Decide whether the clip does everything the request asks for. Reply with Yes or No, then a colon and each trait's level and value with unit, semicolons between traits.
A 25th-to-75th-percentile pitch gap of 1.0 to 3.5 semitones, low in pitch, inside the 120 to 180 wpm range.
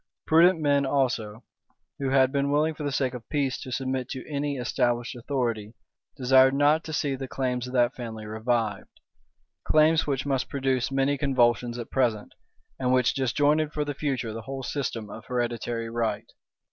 Yes: average, 2.9 semitones; low, 130 Hz; average, 170 wpm